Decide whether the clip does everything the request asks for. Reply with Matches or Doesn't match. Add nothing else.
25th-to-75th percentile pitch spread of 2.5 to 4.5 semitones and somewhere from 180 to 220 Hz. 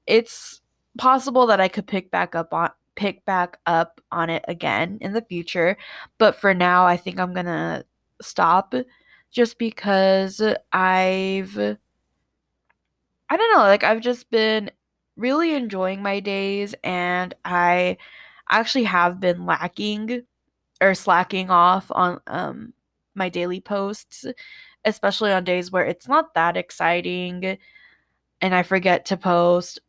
Matches